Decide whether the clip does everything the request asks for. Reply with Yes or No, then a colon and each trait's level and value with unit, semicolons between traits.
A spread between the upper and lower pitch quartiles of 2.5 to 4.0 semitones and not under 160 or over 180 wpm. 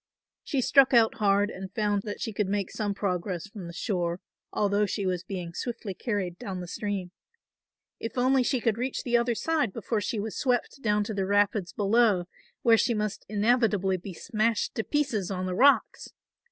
No: average, 3.4 semitones; average, 190 wpm